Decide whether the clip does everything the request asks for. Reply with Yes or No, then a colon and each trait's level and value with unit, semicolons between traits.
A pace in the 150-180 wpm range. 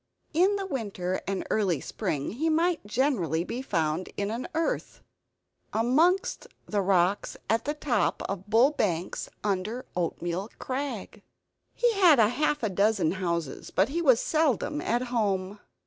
No: average, 140 wpm